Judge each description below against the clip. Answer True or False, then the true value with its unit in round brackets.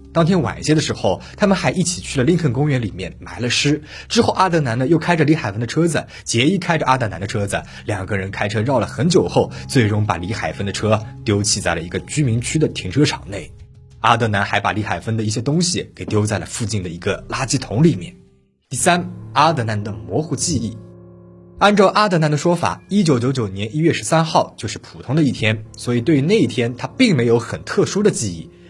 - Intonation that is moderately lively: False (6.9 semitones)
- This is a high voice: False (120 Hz)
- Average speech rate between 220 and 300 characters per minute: False (335 characters per minute)